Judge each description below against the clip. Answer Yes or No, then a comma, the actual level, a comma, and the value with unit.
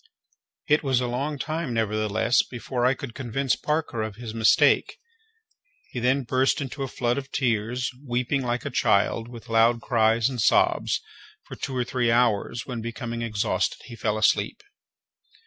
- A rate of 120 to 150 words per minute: No, average, 165 wpm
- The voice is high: No, low, 120 Hz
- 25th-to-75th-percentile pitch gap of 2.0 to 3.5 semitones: Yes, narrow, 2.5 semitones